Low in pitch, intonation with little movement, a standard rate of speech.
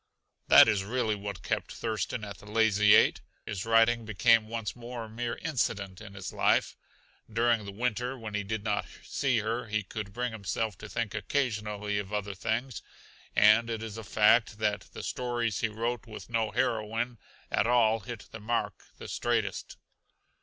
Yes: low, 110 Hz; narrow, 2.0 semitones; average, 175 wpm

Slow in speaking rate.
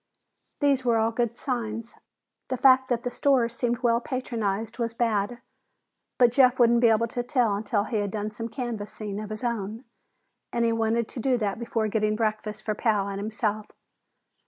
No: average, 180 wpm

